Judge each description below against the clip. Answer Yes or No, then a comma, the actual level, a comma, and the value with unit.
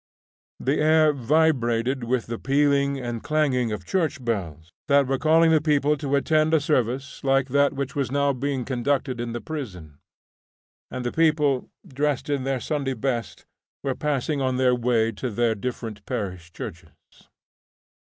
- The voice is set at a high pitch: No, low, 135 Hz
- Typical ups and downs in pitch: Yes, average, 3.3 semitones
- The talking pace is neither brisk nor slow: Yes, average, 160 wpm